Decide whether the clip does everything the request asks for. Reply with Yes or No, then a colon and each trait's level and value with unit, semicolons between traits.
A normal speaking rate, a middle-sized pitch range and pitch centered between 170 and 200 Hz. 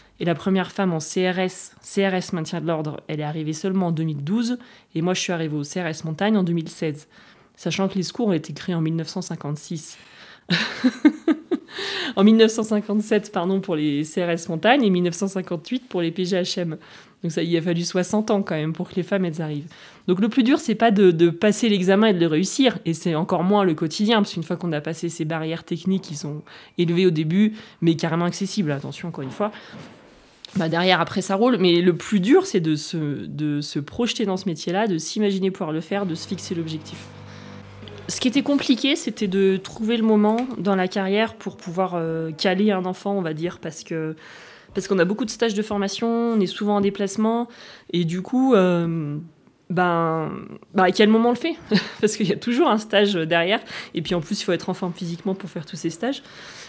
Yes: average, 210 wpm; average, 4.0 semitones; medium, 185 Hz